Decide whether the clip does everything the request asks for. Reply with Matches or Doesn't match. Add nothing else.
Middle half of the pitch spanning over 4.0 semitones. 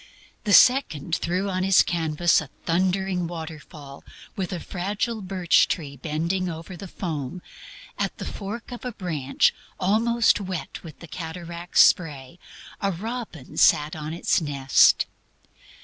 Doesn't match